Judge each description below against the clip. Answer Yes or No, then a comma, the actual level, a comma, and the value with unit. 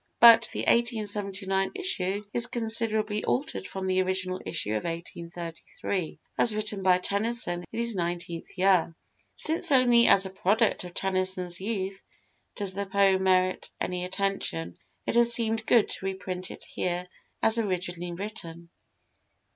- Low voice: No, high, 190 Hz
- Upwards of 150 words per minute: No, average, 140 wpm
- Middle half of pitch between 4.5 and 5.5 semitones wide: No, average, 3.4 semitones